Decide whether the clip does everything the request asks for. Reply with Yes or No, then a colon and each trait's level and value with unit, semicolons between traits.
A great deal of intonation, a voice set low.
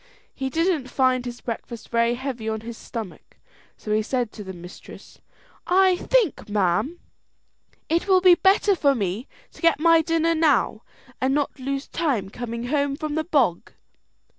No: wide, 6.0 semitones; very high, 265 Hz